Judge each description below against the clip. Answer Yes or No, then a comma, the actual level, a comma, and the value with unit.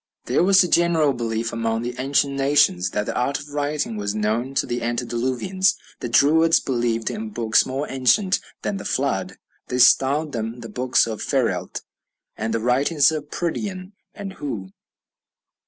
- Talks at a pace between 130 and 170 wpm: Yes, average, 165 wpm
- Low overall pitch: Yes, low, 130 Hz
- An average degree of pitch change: Yes, average, 5.0 semitones